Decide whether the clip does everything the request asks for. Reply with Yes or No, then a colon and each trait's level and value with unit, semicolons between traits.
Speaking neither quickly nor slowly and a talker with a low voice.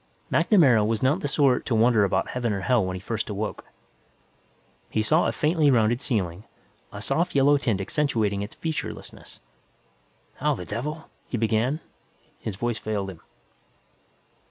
Yes: average, 155 wpm; low, 115 Hz